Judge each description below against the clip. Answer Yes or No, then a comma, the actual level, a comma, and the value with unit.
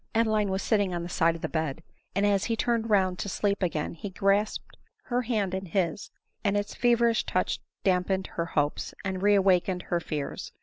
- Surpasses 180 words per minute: Yes, average, 190 wpm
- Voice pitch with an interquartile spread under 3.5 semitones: Yes, average, 2.8 semitones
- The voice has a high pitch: Yes, high, 195 Hz